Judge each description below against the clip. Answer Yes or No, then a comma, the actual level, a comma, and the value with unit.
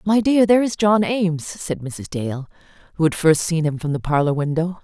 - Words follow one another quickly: Yes, fast, 225 wpm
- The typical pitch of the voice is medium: Yes, medium, 170 Hz